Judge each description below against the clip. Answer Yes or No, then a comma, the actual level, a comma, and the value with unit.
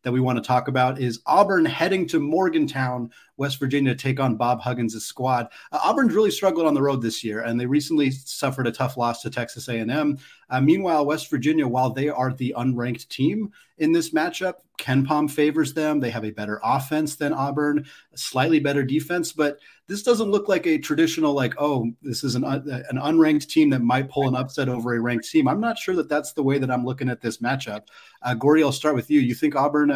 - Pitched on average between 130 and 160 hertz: Yes, medium, 140 Hz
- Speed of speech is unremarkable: No, fast, 225 wpm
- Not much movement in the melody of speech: No, average, 3.5 semitones